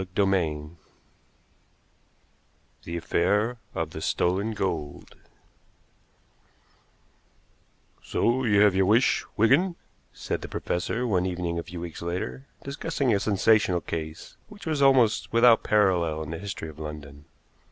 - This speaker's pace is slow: Yes, slow, 125 wpm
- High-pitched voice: No, very low, 95 Hz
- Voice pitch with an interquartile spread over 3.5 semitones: Yes, average, 5.2 semitones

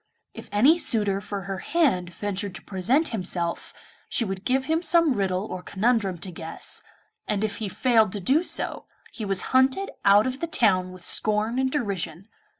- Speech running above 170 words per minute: Yes, average, 180 wpm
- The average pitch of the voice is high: Yes, high, 205 Hz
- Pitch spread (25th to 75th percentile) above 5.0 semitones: Yes, wide, 5.6 semitones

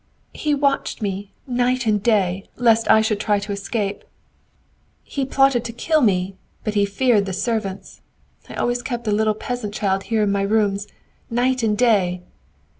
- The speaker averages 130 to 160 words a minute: No, average, 170 wpm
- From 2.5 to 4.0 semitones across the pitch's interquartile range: Yes, average, 3.4 semitones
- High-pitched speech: Yes, high, 215 Hz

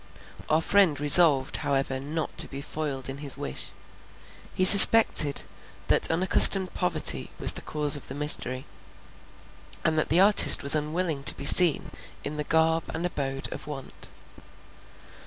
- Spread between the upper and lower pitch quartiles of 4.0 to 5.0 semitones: No, average, 3.1 semitones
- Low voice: No, medium, 150 Hz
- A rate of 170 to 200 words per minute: No, average, 150 wpm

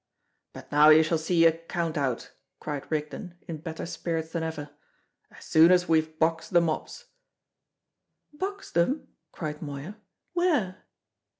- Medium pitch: Yes, medium, 165 Hz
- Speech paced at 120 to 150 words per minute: Yes, average, 140 wpm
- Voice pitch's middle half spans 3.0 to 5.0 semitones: No, narrow, 2.4 semitones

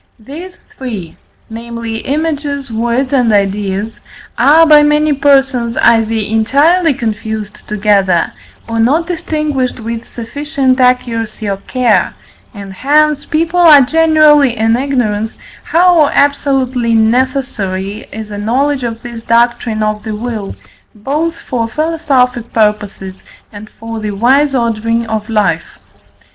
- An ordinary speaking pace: No, slow, 120 wpm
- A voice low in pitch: No, high, 235 Hz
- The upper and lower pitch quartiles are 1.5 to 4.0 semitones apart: No, average, 4.6 semitones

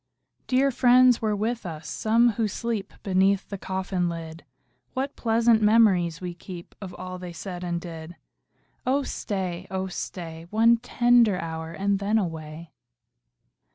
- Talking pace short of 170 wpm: Yes, average, 145 wpm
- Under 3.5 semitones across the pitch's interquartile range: No, average, 4.6 semitones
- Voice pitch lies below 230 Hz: Yes, high, 190 Hz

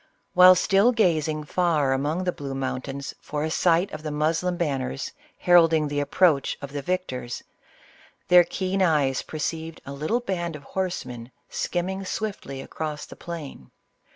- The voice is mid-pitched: Yes, medium, 160 Hz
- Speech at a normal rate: Yes, average, 150 wpm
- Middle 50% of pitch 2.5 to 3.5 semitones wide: No, average, 4.3 semitones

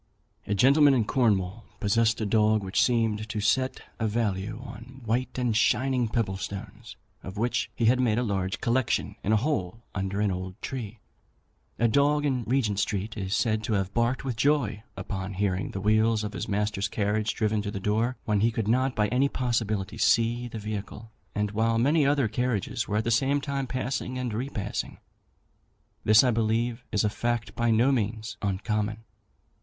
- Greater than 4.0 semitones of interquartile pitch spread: No, average, 2.9 semitones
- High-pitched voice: No, low, 110 Hz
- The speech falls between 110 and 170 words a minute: No, average, 180 wpm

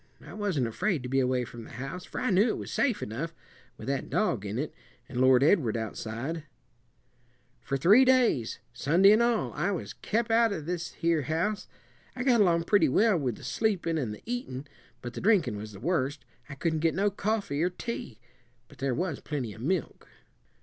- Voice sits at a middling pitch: Yes, medium, 165 Hz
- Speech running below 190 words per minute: No, average, 200 wpm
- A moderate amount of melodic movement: No, wide, 7.9 semitones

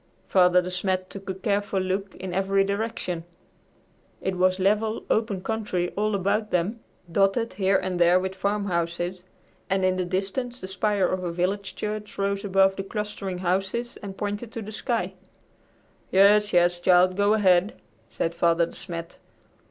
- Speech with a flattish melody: Yes, narrow, 2.1 semitones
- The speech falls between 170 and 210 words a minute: No, average, 160 wpm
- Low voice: No, high, 195 Hz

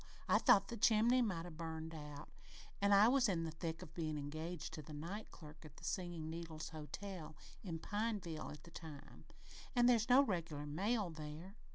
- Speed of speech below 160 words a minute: No, average, 190 wpm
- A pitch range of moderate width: Yes, average, 4.6 semitones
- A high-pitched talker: No, medium, 165 Hz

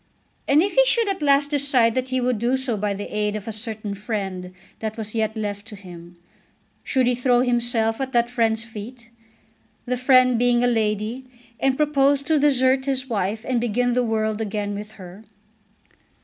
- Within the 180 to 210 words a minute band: Yes, average, 190 wpm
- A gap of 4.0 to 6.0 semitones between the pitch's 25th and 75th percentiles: No, average, 3.4 semitones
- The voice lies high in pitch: Yes, high, 235 Hz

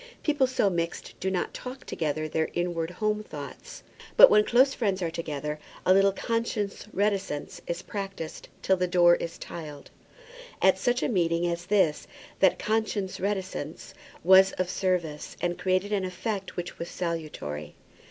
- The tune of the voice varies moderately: Yes, average, 3.3 semitones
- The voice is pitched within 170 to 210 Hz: Yes, medium, 185 Hz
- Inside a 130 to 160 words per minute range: Yes, average, 155 wpm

